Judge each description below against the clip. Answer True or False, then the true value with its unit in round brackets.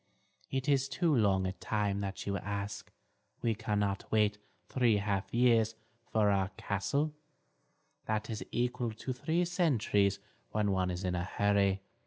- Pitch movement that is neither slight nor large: True (3.6 semitones)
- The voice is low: True (105 Hz)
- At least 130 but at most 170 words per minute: True (150 wpm)